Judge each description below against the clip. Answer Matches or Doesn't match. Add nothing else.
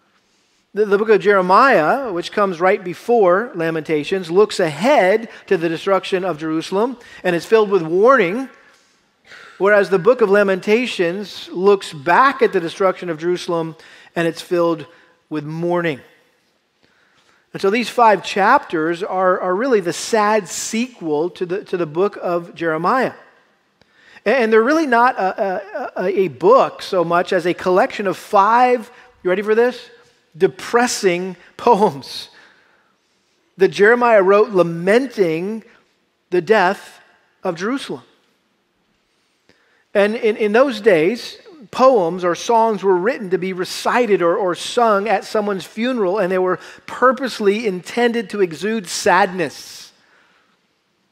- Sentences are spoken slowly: Matches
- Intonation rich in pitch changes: Doesn't match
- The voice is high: Matches